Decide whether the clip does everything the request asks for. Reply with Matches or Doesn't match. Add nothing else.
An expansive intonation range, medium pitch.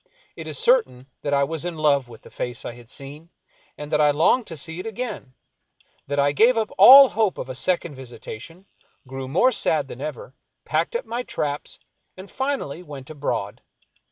Matches